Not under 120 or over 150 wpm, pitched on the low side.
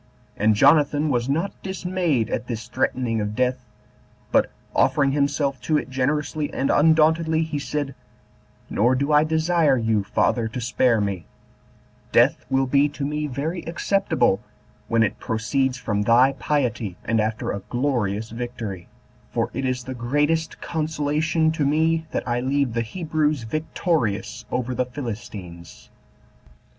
Yes: average, 145 wpm; low, 130 Hz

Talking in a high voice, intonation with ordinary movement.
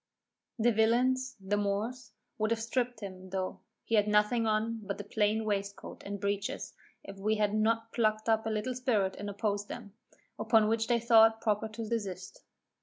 No: high, 215 Hz; narrow, 1.9 semitones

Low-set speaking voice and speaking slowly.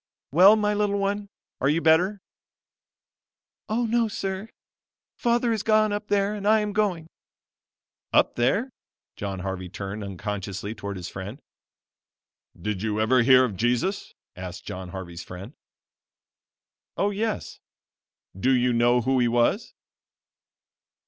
Yes: low, 130 Hz; slow, 130 wpm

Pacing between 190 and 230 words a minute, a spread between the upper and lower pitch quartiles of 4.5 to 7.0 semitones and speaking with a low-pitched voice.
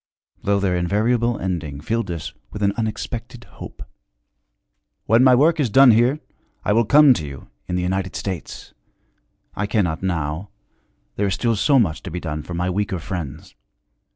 No: average, 170 wpm; average, 5.0 semitones; low, 100 Hz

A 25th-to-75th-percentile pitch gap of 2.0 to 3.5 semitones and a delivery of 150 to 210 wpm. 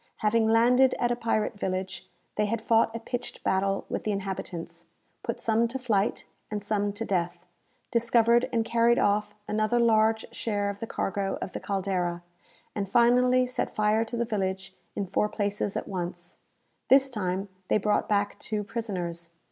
Yes: average, 3.0 semitones; average, 170 wpm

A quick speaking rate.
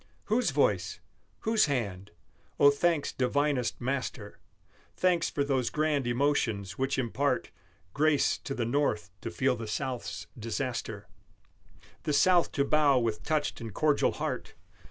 No: slow, 135 wpm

